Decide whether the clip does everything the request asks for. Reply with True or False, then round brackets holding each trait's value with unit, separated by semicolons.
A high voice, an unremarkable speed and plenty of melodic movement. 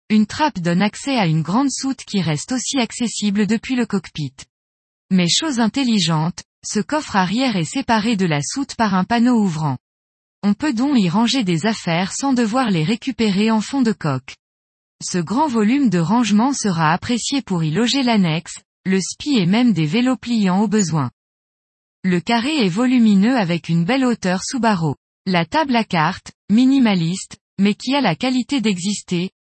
True (215 Hz; 175 wpm; 5.7 semitones)